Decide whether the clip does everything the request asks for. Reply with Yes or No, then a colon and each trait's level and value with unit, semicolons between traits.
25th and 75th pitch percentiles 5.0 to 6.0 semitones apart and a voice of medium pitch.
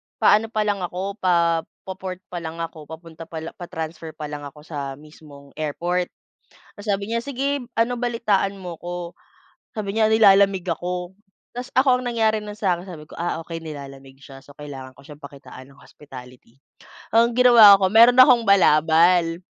Yes: wide, 5.4 semitones; medium, 175 Hz